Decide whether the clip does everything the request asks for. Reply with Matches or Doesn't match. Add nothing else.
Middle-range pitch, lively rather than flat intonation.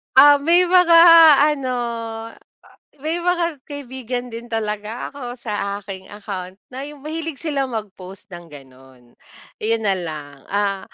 Doesn't match